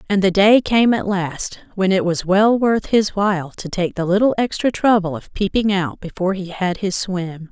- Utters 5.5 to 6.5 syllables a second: No, 4.7 syllables/s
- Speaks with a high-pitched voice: Yes, high, 195 Hz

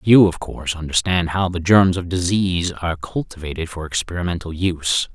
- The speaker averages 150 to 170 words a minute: Yes, average, 165 wpm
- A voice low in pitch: Yes, very low, 85 Hz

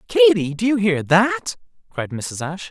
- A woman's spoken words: No, male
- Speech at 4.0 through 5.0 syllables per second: Yes, 4.5 syllables/s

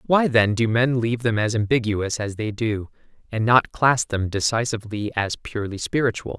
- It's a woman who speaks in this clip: No, male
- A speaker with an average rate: Yes, average, 180 wpm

